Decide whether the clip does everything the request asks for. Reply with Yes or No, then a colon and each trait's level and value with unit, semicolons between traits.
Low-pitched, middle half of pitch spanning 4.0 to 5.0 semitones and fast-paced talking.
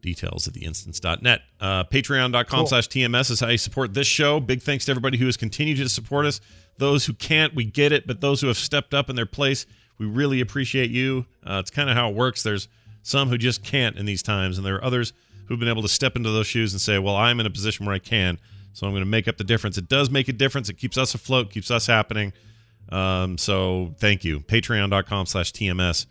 Yes: low, 115 Hz; average, 4.6 semitones; fast, 245 wpm